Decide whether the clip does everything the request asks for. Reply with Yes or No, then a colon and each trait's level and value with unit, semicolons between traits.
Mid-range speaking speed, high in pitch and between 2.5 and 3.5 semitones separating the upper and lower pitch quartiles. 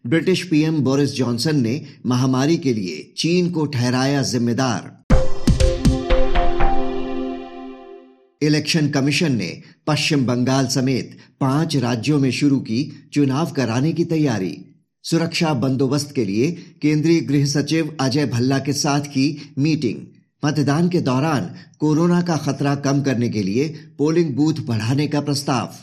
No: average, 130 wpm; medium, 140 Hz; average, 2.8 semitones